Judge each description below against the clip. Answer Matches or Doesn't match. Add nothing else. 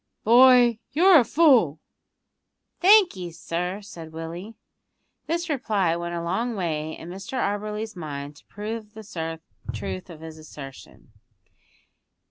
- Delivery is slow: Matches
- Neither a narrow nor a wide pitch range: Doesn't match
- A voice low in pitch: Doesn't match